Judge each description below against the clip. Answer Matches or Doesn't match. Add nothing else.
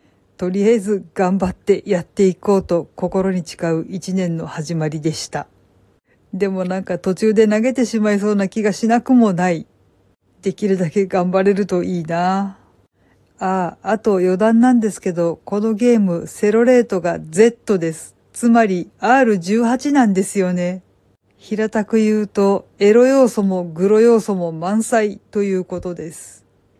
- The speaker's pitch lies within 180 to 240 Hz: Matches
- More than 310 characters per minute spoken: Doesn't match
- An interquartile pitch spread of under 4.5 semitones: Matches